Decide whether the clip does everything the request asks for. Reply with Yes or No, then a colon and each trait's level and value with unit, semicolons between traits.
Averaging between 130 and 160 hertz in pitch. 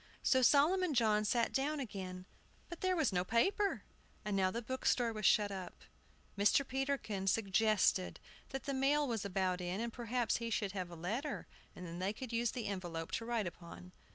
No: high, 220 Hz